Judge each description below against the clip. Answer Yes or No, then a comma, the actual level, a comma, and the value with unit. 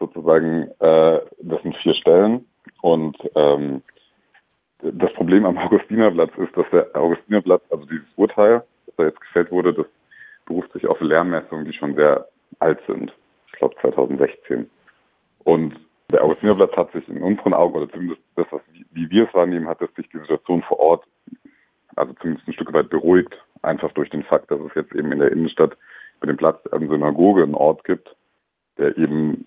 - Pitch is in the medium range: No, low, 110 Hz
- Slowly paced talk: No, average, 180 wpm